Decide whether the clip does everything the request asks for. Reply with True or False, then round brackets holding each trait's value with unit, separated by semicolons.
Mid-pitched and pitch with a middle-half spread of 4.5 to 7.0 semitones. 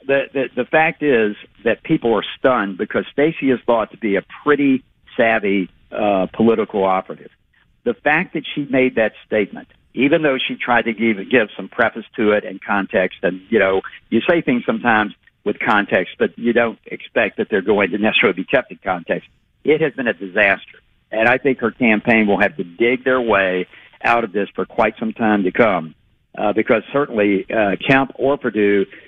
False (115 Hz; 4.8 semitones)